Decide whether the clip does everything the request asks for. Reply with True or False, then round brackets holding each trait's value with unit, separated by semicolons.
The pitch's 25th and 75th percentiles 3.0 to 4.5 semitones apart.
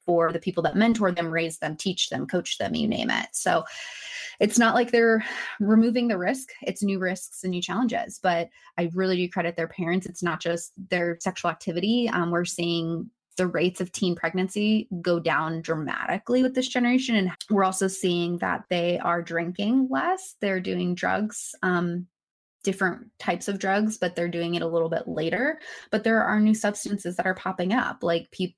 True (4.2 semitones)